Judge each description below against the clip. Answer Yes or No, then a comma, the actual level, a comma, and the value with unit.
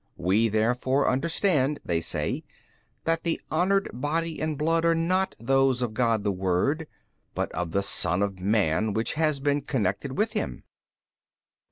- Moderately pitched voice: No, low, 130 Hz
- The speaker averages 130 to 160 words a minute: Yes, average, 155 wpm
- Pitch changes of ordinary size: No, wide, 7.9 semitones